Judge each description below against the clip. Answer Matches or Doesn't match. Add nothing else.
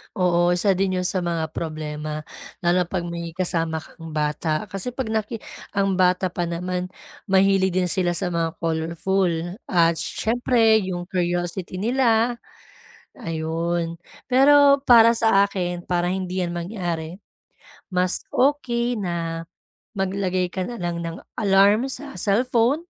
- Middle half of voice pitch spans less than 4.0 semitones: Matches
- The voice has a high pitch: Doesn't match